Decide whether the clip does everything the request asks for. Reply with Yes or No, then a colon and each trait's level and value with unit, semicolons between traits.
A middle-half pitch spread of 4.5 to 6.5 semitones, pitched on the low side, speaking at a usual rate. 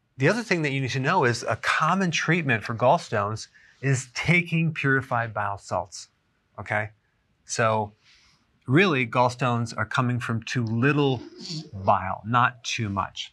Yes: average, 4.9 semitones; low, 125 Hz; average, 145 wpm